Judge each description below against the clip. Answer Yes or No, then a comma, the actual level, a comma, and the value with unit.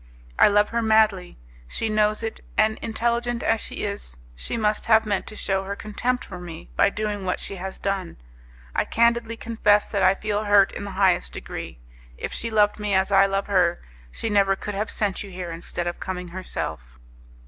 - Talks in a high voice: Yes, high, 205 Hz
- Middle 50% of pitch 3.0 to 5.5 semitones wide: No, narrow, 2.4 semitones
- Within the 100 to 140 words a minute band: No, average, 200 wpm